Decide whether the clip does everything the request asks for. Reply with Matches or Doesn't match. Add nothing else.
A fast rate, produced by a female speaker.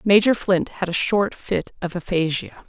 Doesn't match